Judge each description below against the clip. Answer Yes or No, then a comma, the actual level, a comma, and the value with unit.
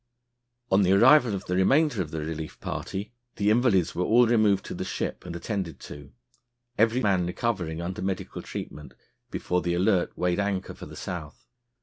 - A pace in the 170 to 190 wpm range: Yes, average, 180 wpm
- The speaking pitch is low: Yes, very low, 95 Hz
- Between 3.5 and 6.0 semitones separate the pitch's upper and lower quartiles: Yes, average, 3.8 semitones